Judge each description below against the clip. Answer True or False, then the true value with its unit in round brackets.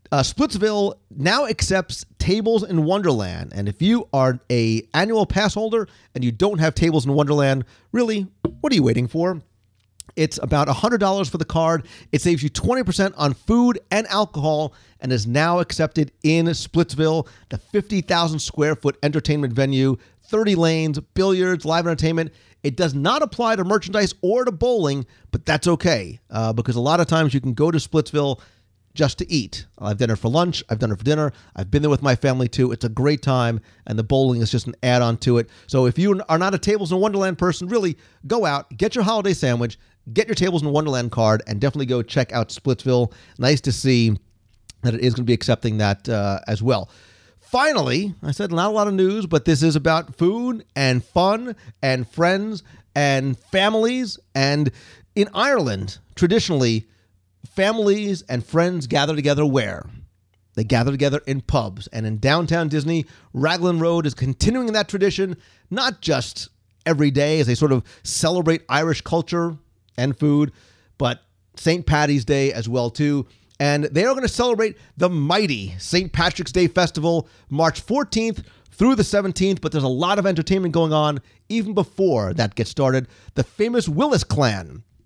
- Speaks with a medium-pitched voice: True (150 Hz)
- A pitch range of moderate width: False (6.8 semitones)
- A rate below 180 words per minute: False (185 wpm)